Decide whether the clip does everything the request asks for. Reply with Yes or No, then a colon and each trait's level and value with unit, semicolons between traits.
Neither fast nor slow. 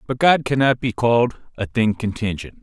Yes: average, 185 wpm